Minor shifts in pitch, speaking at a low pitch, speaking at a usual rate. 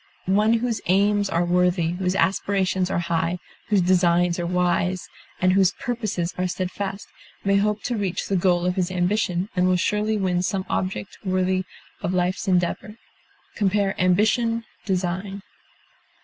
No: narrow, 2.0 semitones; medium, 185 Hz; average, 150 wpm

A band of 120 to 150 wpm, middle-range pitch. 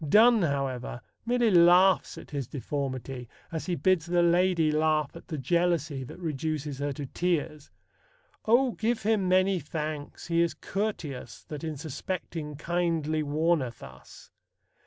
Yes: average, 140 wpm; medium, 160 Hz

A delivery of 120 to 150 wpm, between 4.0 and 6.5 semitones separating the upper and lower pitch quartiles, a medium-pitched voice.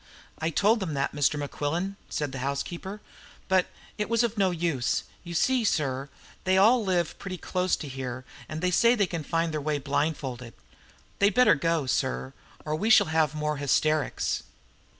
No: average, 175 wpm; average, 4.8 semitones; medium, 160 Hz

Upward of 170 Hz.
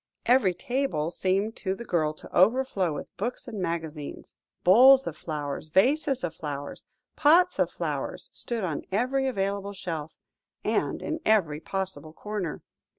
Yes: high, 190 Hz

